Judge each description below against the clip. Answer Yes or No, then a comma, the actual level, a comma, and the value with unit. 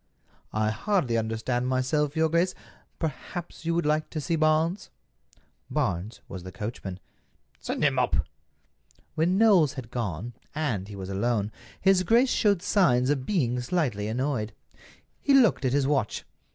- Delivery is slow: No, average, 150 wpm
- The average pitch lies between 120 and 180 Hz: Yes, low, 135 Hz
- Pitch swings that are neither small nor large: No, wide, 7.1 semitones